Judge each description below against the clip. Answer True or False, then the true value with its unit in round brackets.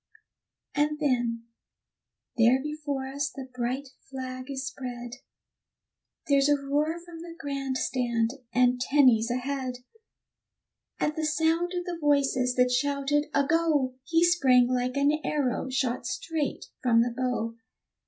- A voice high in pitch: True (270 Hz)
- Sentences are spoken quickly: False (135 wpm)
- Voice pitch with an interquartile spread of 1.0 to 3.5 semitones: True (2.9 semitones)